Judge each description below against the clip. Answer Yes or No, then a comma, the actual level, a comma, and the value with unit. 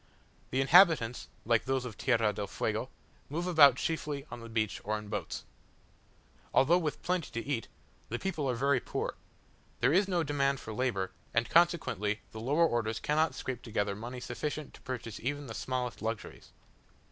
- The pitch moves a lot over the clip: No, average, 4.7 semitones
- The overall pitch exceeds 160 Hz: No, low, 130 Hz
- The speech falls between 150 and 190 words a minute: Yes, average, 170 wpm